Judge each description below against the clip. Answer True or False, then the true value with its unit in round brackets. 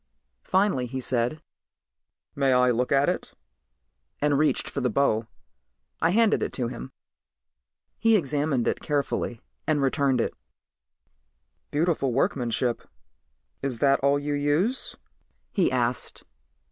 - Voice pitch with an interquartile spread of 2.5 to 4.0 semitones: True (3.0 semitones)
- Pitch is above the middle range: False (140 Hz)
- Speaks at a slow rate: True (120 wpm)